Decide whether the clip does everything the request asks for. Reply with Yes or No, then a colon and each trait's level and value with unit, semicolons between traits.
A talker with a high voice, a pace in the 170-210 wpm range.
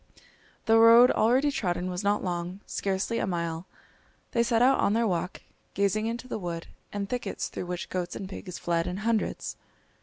Yes: high, 200 Hz; average, 180 wpm